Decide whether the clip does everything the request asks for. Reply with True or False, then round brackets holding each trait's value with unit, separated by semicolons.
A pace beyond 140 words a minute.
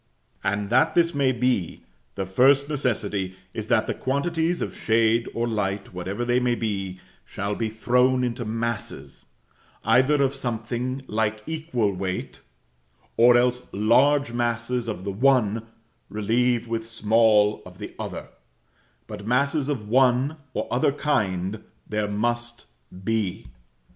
False (135 wpm)